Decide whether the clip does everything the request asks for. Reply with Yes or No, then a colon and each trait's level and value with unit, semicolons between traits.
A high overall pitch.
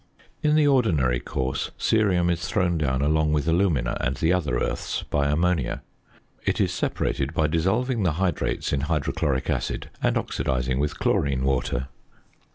No: very low, 75 Hz